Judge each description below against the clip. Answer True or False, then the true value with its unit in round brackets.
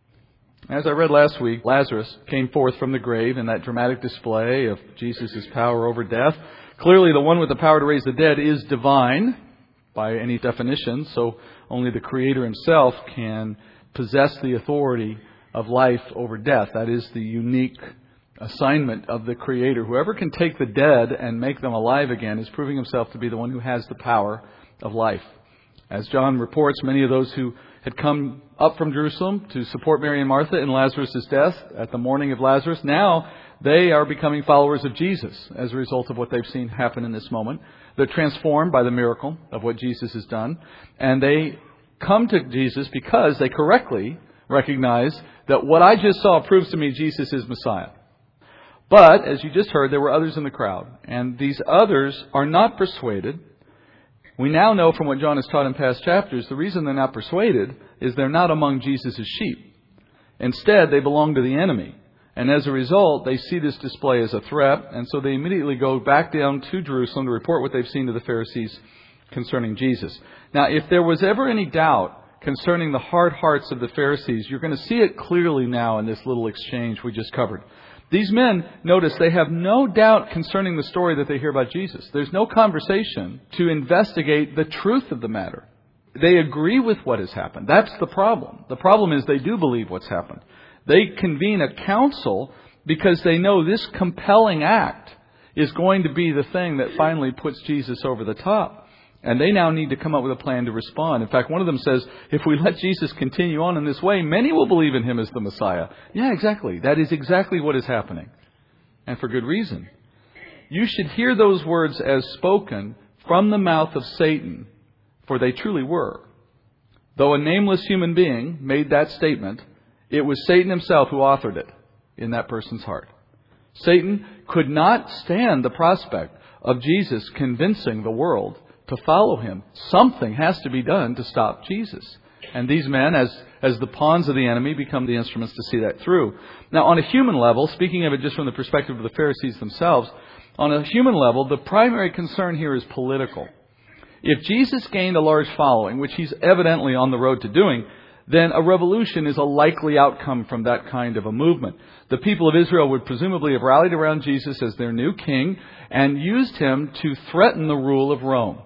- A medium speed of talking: True (195 wpm)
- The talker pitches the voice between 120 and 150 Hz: True (140 Hz)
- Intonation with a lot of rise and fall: False (5.0 semitones)